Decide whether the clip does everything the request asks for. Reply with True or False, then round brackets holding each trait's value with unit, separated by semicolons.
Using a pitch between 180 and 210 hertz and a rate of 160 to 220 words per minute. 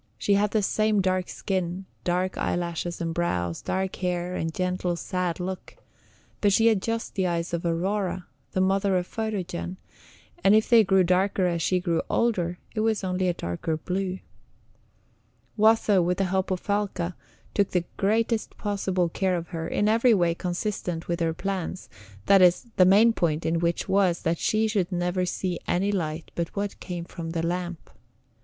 True (185 Hz; 175 wpm)